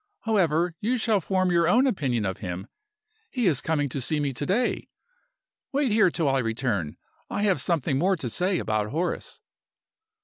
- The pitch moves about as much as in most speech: No, wide, 7.1 semitones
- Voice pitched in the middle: Yes, medium, 165 Hz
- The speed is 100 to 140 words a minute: No, average, 175 wpm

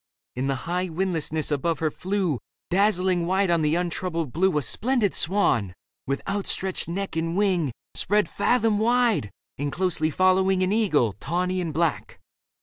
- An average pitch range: Yes, average, 3.6 semitones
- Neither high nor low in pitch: Yes, medium, 180 Hz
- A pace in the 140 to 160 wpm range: Yes, average, 150 wpm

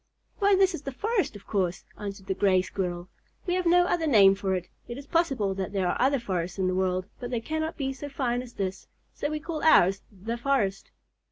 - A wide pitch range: Yes, wide, 7.6 semitones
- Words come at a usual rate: No, fast, 230 wpm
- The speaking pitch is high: Yes, high, 235 Hz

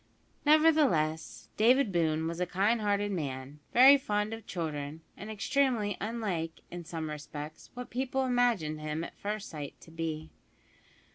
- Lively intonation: Yes, wide, 6.8 semitones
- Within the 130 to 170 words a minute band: Yes, average, 145 wpm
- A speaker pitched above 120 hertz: Yes, high, 190 Hz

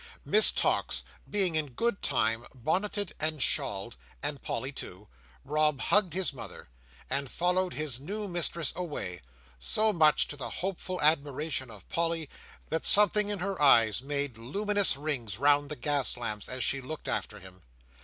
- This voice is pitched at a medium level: Yes, medium, 150 Hz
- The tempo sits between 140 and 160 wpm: Yes, average, 155 wpm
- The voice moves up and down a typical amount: No, wide, 5.8 semitones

